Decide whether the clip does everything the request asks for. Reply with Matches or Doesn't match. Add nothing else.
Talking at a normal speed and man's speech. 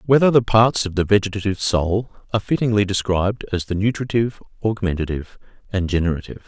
Matches